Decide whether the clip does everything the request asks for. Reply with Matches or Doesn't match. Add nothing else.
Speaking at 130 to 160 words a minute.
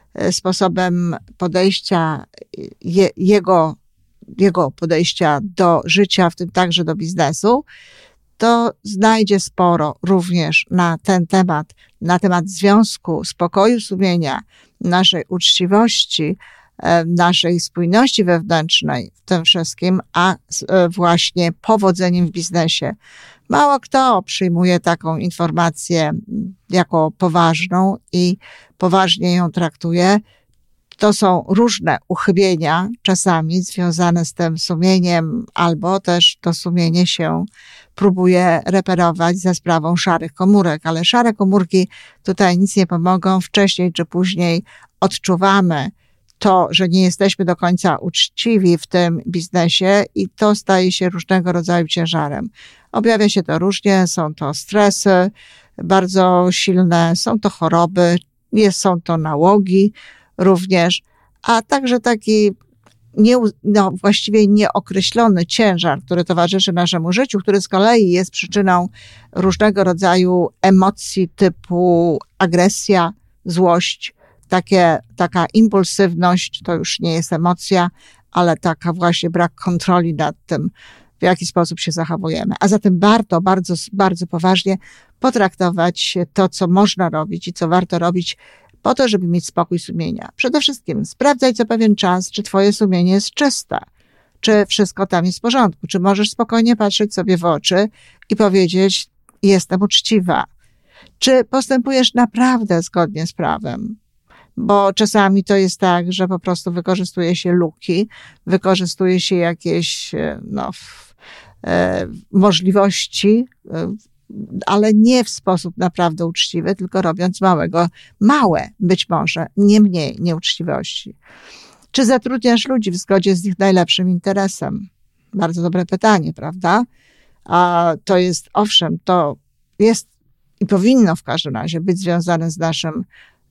Doesn't match